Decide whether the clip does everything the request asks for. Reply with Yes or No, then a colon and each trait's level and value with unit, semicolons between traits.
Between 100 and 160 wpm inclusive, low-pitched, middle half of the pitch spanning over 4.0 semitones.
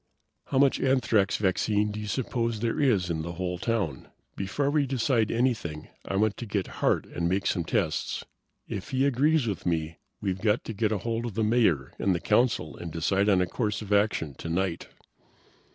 No: average, 190 wpm; low, 105 Hz; average, 4.6 semitones